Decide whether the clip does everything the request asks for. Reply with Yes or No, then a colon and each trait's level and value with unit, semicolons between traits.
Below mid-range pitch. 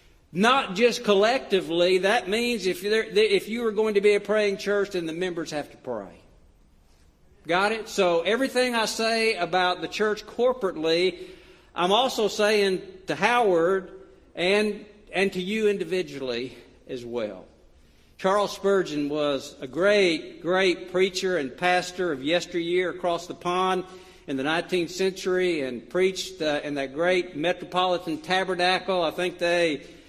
No: medium, 185 Hz